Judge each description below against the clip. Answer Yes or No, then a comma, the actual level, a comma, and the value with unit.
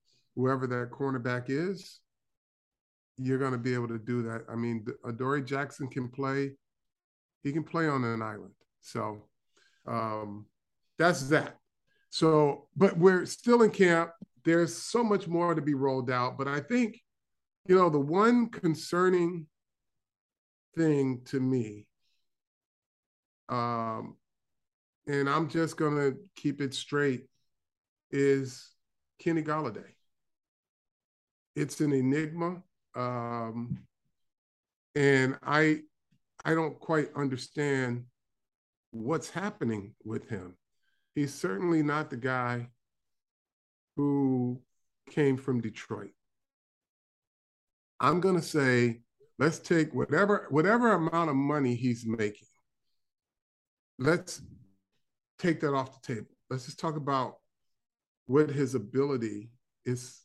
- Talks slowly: Yes, slow, 115 wpm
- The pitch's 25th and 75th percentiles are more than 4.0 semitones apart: Yes, average, 4.8 semitones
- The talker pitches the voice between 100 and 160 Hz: Yes, medium, 140 Hz